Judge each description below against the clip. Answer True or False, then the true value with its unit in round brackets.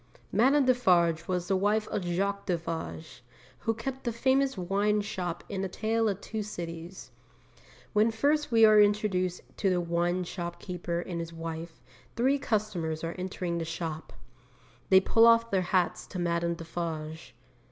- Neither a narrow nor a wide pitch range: True (4.1 semitones)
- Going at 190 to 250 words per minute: False (155 wpm)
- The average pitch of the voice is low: False (185 Hz)